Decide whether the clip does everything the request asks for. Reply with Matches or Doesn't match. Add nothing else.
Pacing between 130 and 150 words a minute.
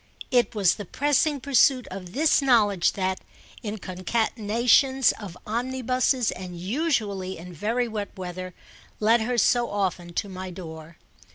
Matches